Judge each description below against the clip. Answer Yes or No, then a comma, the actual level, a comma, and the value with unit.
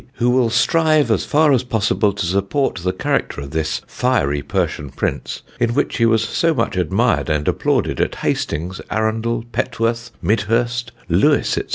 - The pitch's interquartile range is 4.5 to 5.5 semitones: Yes, average, 4.8 semitones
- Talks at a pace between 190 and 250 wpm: No, average, 165 wpm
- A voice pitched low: Yes, low, 115 Hz